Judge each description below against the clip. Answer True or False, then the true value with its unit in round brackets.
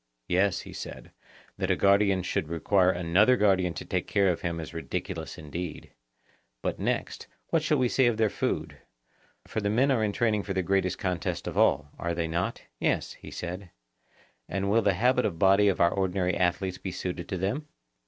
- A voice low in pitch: True (95 Hz)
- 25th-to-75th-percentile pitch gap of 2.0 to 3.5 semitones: True (2.8 semitones)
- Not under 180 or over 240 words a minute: True (195 wpm)